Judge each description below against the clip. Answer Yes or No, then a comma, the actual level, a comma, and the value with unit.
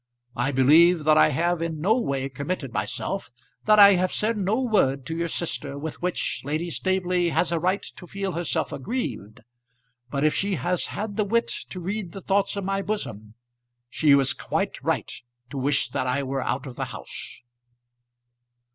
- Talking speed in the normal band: Yes, average, 180 wpm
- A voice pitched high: No, medium, 170 Hz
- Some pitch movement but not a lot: No, wide, 5.9 semitones